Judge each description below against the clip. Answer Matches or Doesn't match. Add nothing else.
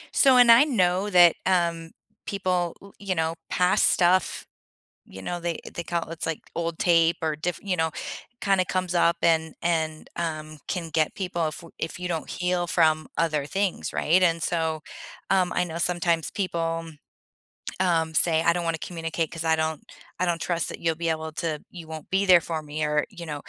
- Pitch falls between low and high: Matches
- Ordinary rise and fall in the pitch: Doesn't match